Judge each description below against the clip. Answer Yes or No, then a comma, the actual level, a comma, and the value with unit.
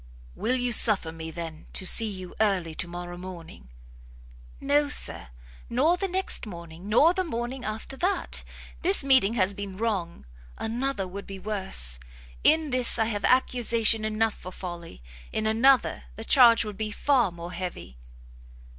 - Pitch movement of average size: No, wide, 5.8 semitones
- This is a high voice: Yes, high, 215 Hz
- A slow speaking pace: No, average, 155 wpm